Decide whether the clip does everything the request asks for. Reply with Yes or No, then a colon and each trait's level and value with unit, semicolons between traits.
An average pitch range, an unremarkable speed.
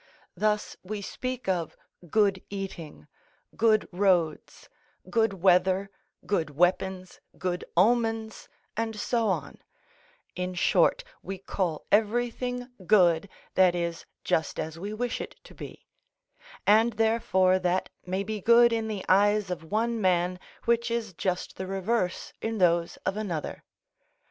No: average, 3.6 semitones; slow, 130 wpm